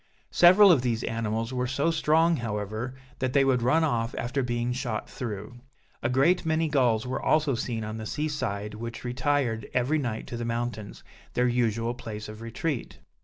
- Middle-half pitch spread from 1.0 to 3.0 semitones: No, average, 3.7 semitones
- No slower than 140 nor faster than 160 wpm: No, average, 180 wpm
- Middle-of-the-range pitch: No, low, 120 Hz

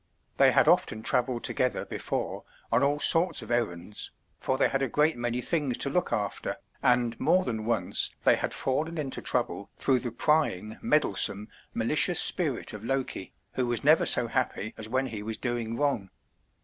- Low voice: Yes, low, 125 Hz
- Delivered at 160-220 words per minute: Yes, average, 175 wpm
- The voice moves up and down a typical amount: Yes, average, 3.9 semitones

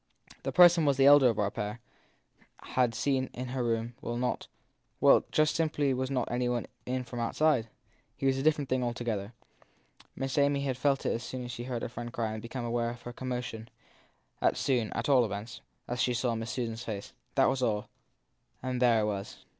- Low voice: Yes, low, 125 Hz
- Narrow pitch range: Yes, narrow, 2.3 semitones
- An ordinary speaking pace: No, fast, 210 wpm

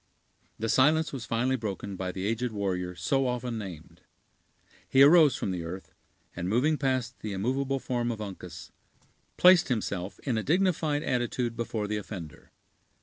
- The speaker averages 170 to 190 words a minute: No, average, 155 wpm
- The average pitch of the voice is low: Yes, low, 115 Hz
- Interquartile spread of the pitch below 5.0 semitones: No, average, 5.3 semitones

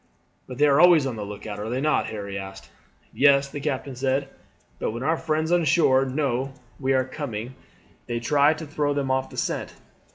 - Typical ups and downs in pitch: Yes, average, 3.5 semitones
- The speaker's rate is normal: No, fast, 215 wpm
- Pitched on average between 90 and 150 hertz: Yes, low, 135 Hz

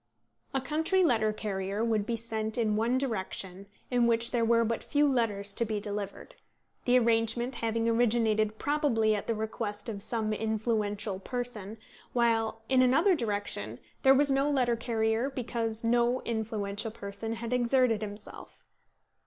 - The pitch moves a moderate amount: No, narrow, 2.2 semitones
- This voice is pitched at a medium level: No, high, 225 Hz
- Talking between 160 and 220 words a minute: No, average, 150 wpm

